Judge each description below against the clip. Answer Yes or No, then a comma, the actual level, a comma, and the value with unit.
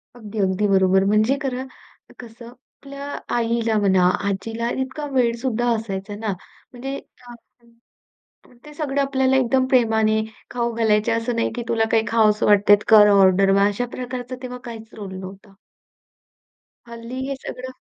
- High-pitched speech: Yes, high, 230 Hz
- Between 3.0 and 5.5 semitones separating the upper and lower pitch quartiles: Yes, average, 3.5 semitones